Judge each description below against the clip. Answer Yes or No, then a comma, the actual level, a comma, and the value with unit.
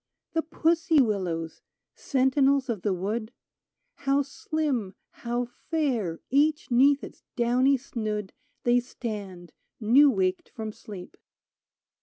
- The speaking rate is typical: No, slow, 120 wpm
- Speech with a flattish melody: No, average, 5.0 semitones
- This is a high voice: Yes, high, 245 Hz